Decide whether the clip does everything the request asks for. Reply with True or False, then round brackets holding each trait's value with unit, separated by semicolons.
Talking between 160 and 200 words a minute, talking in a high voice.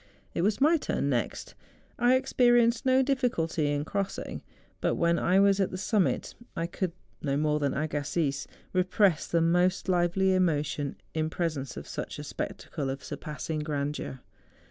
False (165 wpm; 170 Hz)